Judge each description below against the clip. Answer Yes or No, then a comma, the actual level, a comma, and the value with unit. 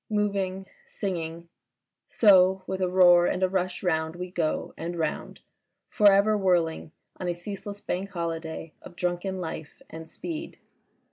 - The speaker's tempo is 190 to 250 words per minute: No, average, 145 wpm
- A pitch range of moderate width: No, narrow, 2.3 semitones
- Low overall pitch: No, medium, 180 Hz